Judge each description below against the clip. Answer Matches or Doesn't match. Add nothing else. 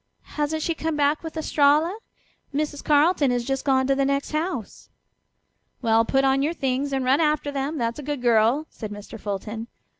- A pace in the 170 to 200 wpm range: Matches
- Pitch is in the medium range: Doesn't match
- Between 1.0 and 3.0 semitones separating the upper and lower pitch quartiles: Doesn't match